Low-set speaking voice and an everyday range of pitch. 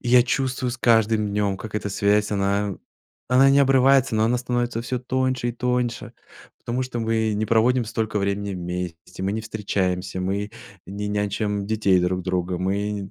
Yes: low, 105 Hz; average, 3.5 semitones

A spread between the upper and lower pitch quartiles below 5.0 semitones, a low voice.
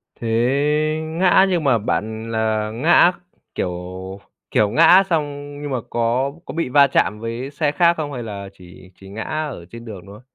No: wide, 5.6 semitones; low, 125 Hz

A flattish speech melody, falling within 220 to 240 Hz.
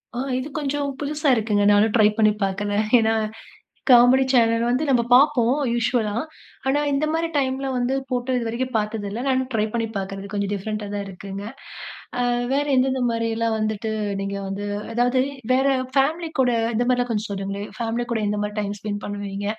No: average, 3.9 semitones; high, 230 Hz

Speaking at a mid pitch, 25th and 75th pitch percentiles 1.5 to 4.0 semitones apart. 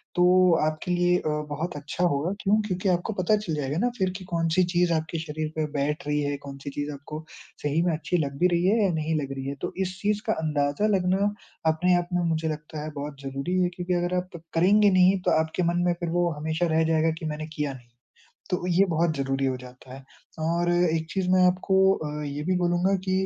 Yes: medium, 170 Hz; average, 3.3 semitones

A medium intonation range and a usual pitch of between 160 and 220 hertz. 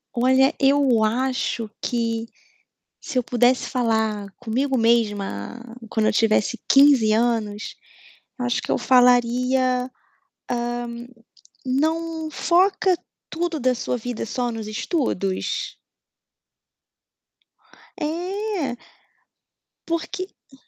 No: average, 4.0 semitones; very high, 250 Hz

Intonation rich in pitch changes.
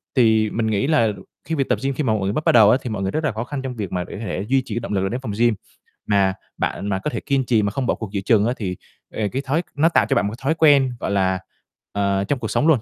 No: average, 5.0 semitones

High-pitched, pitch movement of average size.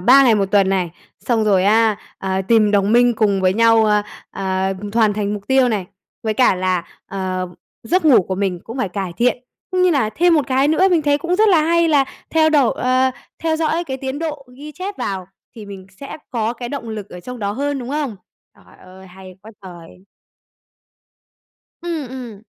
No: high, 230 Hz; wide, 6.6 semitones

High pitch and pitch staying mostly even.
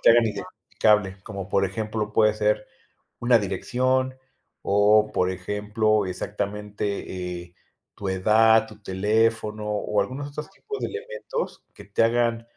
No: low, 105 Hz; narrow, 2.2 semitones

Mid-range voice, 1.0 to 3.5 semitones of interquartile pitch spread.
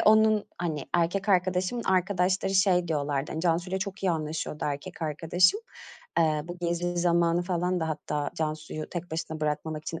Yes: medium, 175 Hz; average, 2.8 semitones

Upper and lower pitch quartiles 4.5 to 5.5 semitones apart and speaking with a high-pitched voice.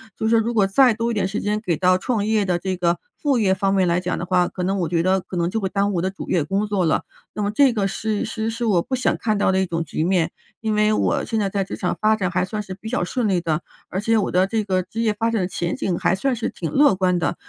No: average, 3.2 semitones; high, 195 Hz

